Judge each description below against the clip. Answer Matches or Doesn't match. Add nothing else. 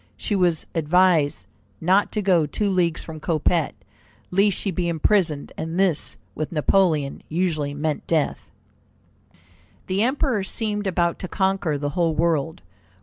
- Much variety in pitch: Doesn't match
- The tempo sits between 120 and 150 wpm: Matches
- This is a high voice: Doesn't match